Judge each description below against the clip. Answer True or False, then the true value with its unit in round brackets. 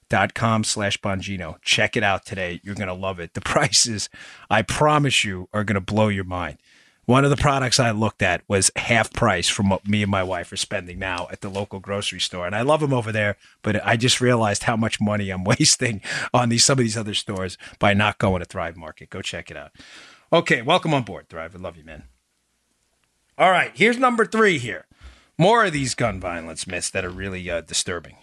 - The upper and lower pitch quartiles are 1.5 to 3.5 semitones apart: False (4.4 semitones)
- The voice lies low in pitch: True (105 Hz)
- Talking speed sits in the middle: False (220 wpm)